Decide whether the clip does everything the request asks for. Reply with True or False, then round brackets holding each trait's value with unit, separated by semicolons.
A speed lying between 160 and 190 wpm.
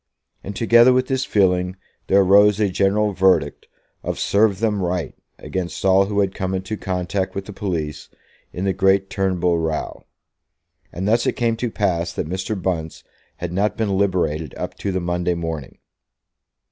True (170 wpm)